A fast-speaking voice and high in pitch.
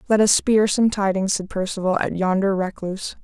No: average, 185 wpm; high, 195 Hz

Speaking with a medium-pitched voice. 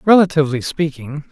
Yes: medium, 150 Hz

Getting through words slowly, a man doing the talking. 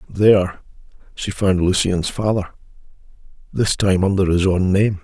Yes: slow, 130 wpm; male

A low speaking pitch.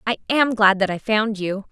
No: high, 210 Hz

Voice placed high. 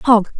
Yes: high, 225 Hz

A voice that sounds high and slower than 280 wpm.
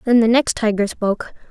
Yes: high, 225 Hz; average, 200 wpm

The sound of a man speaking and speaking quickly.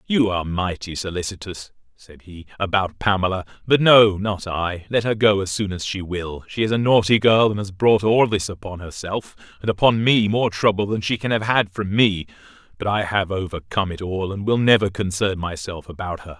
Yes: male; fast, 210 wpm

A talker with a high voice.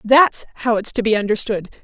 Yes: high, 225 Hz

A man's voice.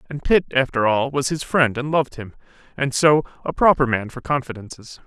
Yes: male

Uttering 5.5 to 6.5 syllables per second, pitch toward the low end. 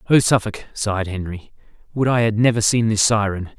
Yes: 5.6 syllables/s; low, 110 Hz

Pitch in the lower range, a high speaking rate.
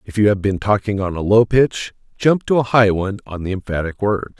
Yes: low, 105 Hz; fast, 245 wpm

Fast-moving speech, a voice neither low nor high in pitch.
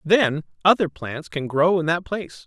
No: average, 195 wpm; medium, 165 Hz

